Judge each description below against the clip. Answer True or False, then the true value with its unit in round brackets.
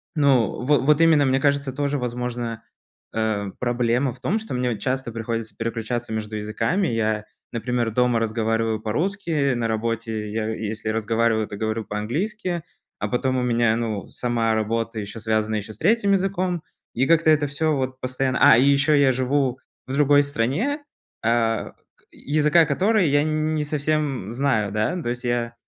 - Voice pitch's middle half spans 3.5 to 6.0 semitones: True (4.4 semitones)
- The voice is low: True (125 Hz)